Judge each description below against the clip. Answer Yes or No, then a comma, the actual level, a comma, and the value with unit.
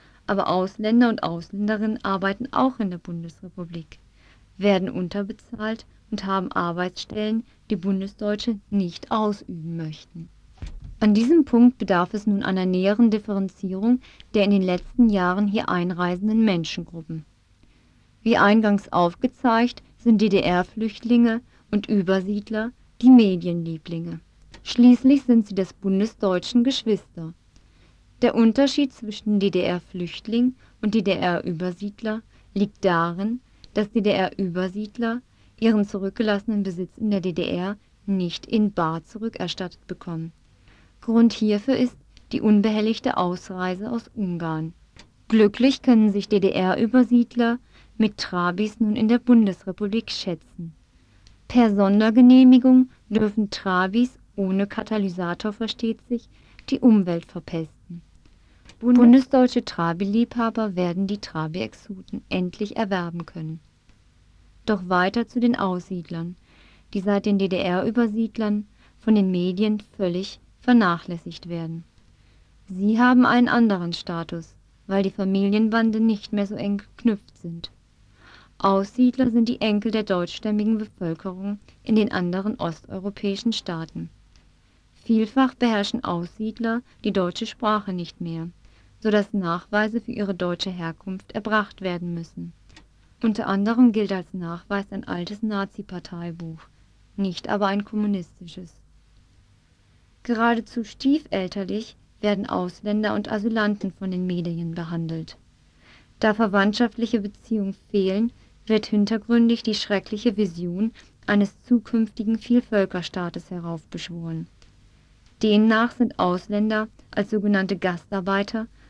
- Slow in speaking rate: Yes, slow, 105 wpm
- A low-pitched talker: No, high, 200 Hz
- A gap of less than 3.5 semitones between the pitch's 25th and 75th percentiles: No, average, 3.9 semitones